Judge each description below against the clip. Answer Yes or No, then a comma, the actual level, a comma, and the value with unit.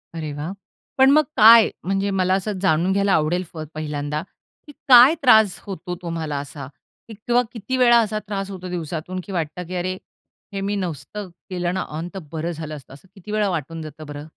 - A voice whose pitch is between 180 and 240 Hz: Yes, medium, 185 Hz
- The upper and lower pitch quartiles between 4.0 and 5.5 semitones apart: Yes, average, 4.5 semitones